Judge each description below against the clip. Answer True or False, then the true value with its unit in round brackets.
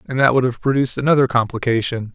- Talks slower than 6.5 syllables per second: False (7.1 syllables/s)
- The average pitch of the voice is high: False (125 Hz)